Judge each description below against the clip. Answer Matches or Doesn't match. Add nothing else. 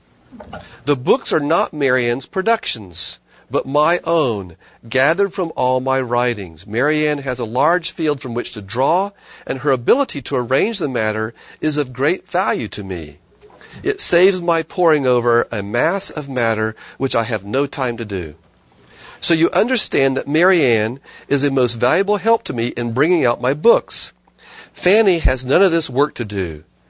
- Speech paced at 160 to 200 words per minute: Matches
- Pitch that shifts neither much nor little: Doesn't match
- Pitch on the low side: Matches